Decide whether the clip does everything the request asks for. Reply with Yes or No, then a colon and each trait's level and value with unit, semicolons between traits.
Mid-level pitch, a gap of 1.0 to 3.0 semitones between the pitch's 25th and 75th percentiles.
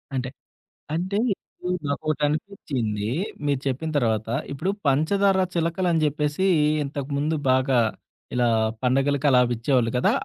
No: medium, 145 Hz; average, 4.0 semitones